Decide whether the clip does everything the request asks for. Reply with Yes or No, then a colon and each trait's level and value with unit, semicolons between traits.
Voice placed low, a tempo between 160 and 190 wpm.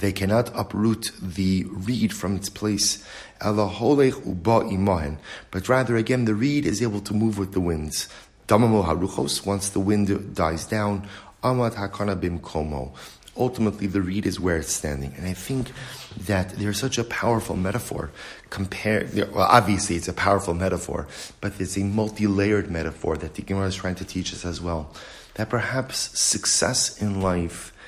No: low, 100 Hz; average, 145 wpm